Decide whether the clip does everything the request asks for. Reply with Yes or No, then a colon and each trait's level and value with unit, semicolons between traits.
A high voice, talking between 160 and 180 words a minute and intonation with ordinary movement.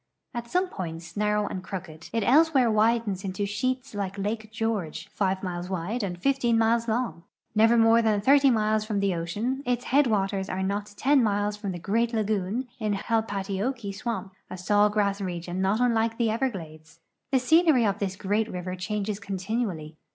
Yes: high, 210 Hz; average, 175 wpm; average, 3.3 semitones